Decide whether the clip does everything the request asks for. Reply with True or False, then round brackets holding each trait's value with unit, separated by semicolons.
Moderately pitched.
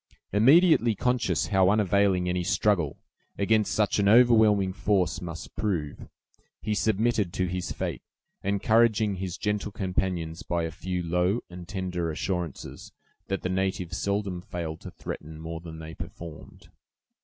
False (95 Hz)